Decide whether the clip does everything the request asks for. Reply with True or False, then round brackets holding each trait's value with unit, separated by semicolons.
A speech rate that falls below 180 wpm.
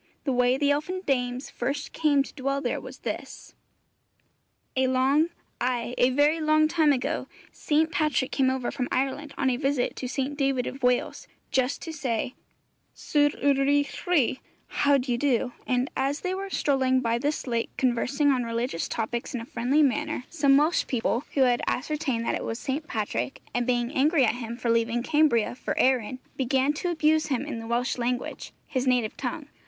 False (185 wpm)